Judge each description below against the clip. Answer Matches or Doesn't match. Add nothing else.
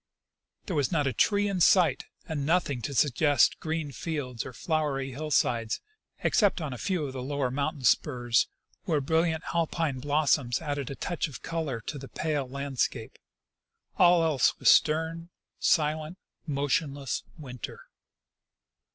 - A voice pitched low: Doesn't match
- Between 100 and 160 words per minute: Matches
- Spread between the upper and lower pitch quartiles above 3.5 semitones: Doesn't match